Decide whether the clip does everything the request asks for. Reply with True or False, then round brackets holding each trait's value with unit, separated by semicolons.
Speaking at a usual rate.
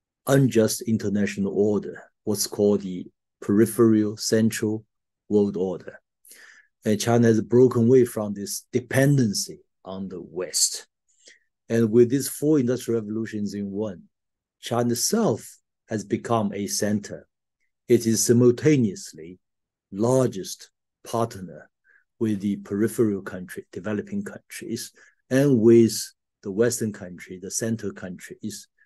False (110 wpm)